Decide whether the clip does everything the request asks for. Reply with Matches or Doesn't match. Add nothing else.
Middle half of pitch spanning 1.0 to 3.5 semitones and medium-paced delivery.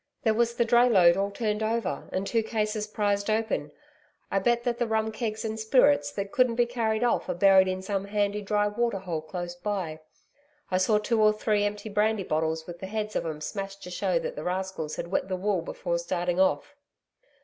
Doesn't match